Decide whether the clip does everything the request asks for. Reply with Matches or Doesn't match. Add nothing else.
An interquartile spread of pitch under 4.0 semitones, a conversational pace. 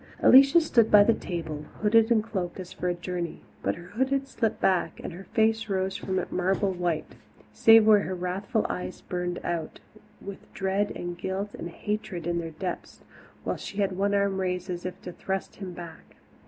Matches